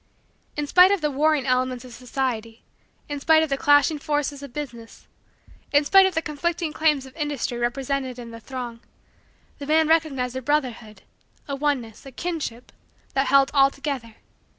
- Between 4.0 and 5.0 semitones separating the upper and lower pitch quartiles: No, average, 3.2 semitones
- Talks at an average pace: Yes, average, 170 wpm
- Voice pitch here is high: Yes, very high, 275 Hz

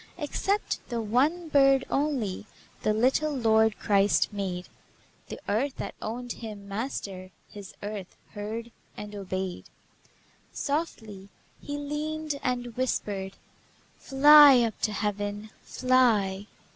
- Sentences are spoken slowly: Yes, slow, 110 wpm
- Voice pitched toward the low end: No, high, 225 Hz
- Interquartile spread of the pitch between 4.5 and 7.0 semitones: Yes, average, 5.0 semitones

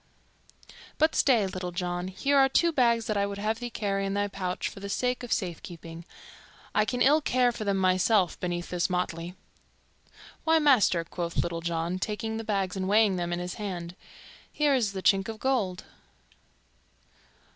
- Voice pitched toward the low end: No, high, 195 Hz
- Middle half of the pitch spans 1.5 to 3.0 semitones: No, average, 4.3 semitones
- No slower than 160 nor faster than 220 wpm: Yes, average, 180 wpm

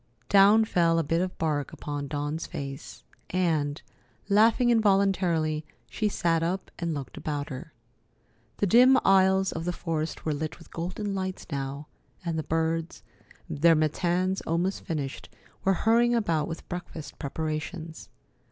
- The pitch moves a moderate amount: Yes, average, 3.7 semitones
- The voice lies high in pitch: No, medium, 165 Hz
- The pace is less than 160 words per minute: Yes, average, 145 wpm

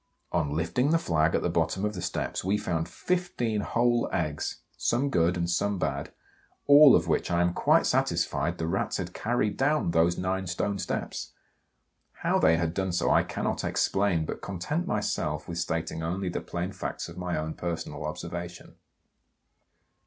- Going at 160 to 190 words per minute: Yes, average, 175 wpm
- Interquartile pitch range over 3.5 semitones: Yes, average, 4.0 semitones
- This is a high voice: No, very low, 90 Hz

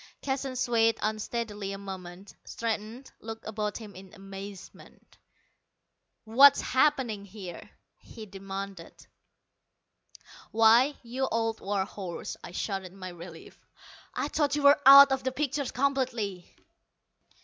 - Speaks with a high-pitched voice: Yes, high, 220 Hz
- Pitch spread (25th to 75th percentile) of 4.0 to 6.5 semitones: Yes, average, 4.9 semitones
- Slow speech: Yes, slow, 120 wpm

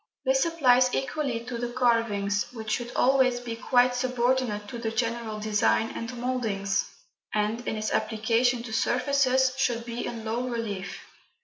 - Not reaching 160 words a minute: Yes, average, 150 wpm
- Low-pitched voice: No, high, 235 Hz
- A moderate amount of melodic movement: No, narrow, 2.3 semitones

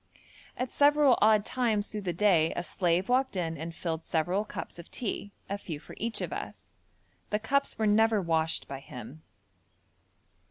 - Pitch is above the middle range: Yes, high, 200 Hz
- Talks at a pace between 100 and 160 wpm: No, average, 170 wpm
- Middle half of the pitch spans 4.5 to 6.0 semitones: Yes, average, 5.3 semitones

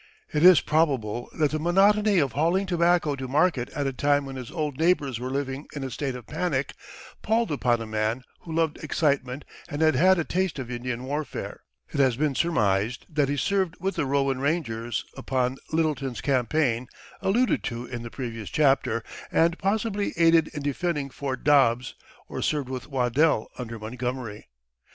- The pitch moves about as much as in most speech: Yes, average, 4.5 semitones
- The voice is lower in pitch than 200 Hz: Yes, medium, 140 Hz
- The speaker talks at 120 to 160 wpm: No, average, 175 wpm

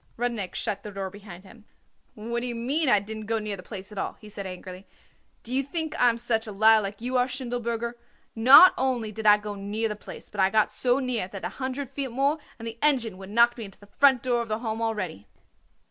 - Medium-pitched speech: No, high, 225 Hz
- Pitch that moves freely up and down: No, average, 3.2 semitones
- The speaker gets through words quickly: Yes, fast, 245 wpm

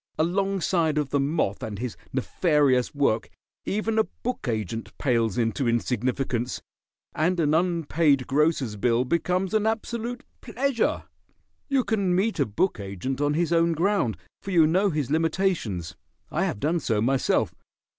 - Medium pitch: Yes, medium, 155 Hz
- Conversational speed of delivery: Yes, average, 145 wpm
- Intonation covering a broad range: Yes, wide, 6.9 semitones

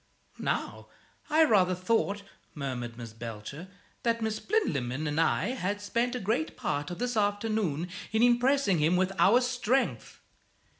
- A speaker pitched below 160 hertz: No, high, 205 Hz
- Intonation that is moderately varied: No, wide, 7.6 semitones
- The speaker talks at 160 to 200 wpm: No, average, 145 wpm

